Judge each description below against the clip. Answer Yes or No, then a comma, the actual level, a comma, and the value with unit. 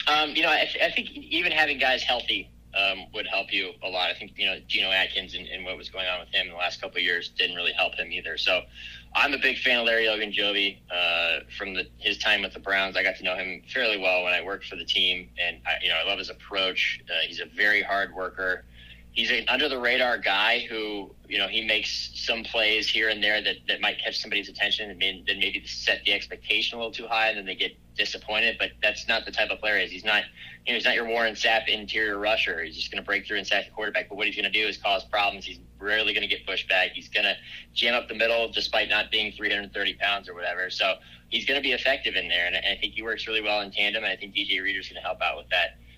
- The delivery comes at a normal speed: No, fast, 275 wpm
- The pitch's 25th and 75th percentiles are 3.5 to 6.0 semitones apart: No, average, 3.1 semitones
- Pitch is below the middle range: Yes, low, 105 Hz